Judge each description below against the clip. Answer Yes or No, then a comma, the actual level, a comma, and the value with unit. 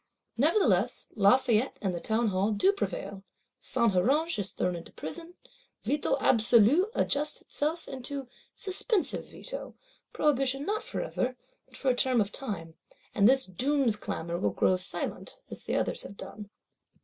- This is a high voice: Yes, very high, 250 Hz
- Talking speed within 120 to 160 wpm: Yes, average, 145 wpm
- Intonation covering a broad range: Yes, wide, 6.4 semitones